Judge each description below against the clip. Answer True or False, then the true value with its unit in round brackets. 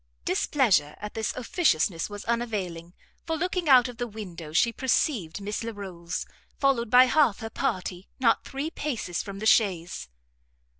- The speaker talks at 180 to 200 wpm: False (150 wpm)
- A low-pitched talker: False (220 Hz)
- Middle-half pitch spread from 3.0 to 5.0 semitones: False (5.5 semitones)